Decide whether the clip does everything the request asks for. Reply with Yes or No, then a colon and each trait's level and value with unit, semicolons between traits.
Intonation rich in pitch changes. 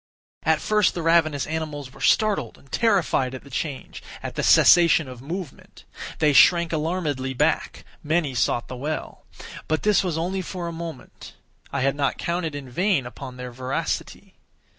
No: average, 4.4 semitones